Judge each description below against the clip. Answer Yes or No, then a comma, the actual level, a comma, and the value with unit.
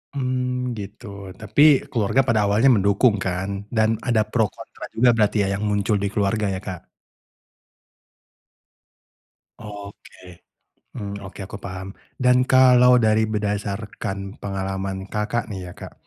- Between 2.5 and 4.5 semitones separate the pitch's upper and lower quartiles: Yes, average, 3.3 semitones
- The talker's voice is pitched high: No, low, 105 Hz